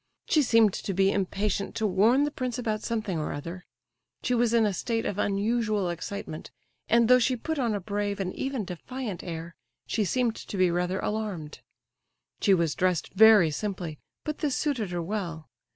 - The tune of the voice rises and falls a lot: No, average, 4.3 semitones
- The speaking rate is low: No, average, 185 wpm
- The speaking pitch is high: Yes, high, 205 Hz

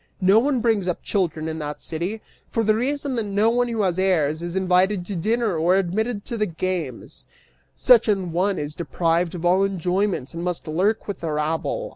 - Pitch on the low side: No, medium, 185 Hz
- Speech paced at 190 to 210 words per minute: Yes, average, 200 wpm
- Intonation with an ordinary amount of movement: Yes, average, 4.2 semitones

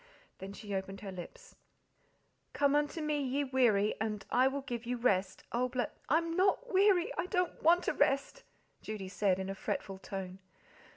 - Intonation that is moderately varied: No, wide, 7.4 semitones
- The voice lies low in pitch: No, very high, 250 Hz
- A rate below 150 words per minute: No, average, 175 wpm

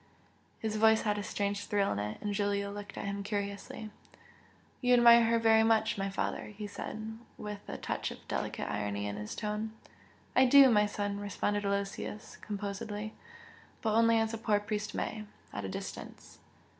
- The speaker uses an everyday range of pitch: No, narrow, 1.7 semitones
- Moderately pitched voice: No, high, 210 Hz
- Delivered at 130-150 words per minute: No, average, 175 wpm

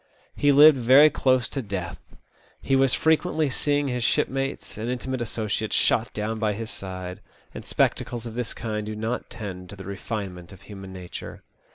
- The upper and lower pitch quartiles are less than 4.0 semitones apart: No, average, 4.8 semitones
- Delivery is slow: No, average, 175 wpm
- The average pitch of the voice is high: No, low, 115 Hz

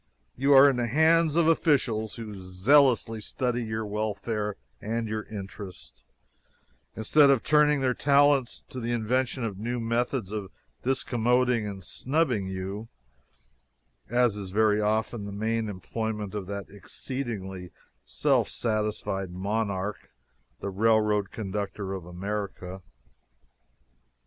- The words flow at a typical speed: No, slow, 120 wpm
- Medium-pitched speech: No, low, 110 Hz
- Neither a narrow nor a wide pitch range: Yes, average, 3.6 semitones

